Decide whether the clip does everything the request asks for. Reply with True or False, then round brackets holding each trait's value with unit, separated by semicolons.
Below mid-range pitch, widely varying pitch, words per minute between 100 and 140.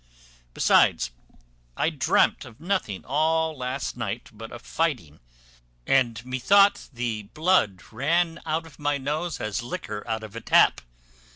True (130 Hz; 6.2 semitones; 135 wpm)